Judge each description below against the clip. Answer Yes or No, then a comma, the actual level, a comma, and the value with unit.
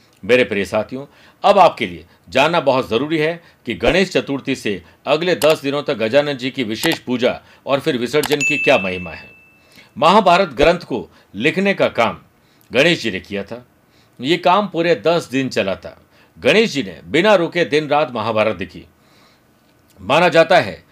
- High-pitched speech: No, medium, 140 Hz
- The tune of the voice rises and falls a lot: Yes, wide, 6.4 semitones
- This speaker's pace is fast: No, average, 170 wpm